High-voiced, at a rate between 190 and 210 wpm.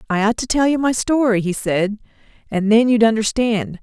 Yes: high, 225 Hz; fast, 205 wpm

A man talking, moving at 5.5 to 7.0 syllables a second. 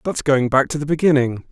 Yes: male; 5.8 syllables/s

